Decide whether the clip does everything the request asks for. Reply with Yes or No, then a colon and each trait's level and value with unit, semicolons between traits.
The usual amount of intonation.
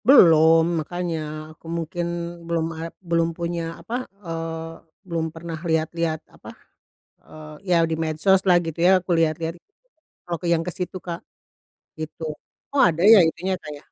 No: narrow, 1.4 semitones